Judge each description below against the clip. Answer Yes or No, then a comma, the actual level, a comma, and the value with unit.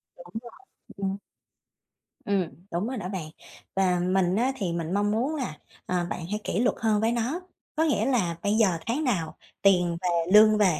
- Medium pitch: No, high, 200 Hz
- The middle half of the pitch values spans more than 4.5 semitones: No, average, 4.2 semitones